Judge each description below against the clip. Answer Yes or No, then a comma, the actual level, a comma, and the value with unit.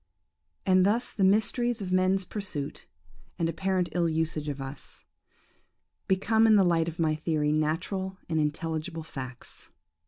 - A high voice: No, medium, 175 Hz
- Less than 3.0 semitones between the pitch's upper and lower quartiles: No, average, 3.7 semitones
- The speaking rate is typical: Yes, average, 145 wpm